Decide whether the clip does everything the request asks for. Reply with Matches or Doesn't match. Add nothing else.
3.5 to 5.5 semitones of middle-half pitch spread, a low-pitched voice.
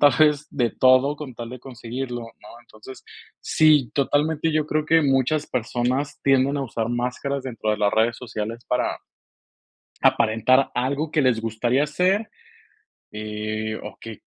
Matches